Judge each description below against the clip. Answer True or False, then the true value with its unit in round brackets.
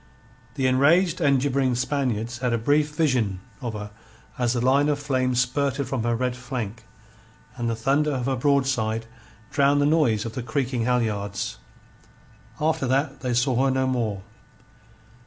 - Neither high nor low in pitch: False (130 Hz)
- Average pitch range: True (3.0 semitones)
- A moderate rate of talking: True (160 wpm)